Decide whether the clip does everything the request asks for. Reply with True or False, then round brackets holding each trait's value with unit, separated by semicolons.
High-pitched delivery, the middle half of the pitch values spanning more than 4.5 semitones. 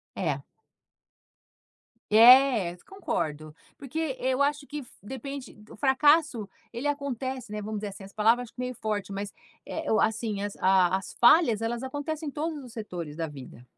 True (235 Hz; 5.5 semitones)